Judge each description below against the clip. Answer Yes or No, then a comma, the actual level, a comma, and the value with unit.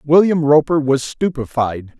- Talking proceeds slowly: Yes, slow, 120 wpm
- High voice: No, medium, 145 Hz